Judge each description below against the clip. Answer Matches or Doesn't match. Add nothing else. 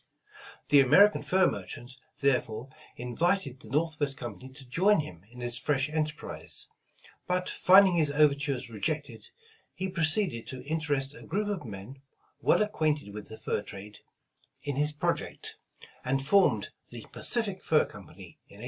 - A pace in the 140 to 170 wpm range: Matches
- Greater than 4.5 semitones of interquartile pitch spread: Matches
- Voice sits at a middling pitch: Matches